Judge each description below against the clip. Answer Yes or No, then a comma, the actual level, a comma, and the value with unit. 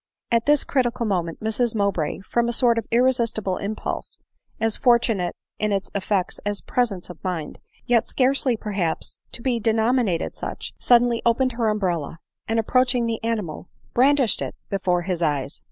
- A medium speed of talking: Yes, average, 155 wpm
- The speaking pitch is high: Yes, high, 220 Hz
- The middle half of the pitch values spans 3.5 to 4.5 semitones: Yes, average, 3.9 semitones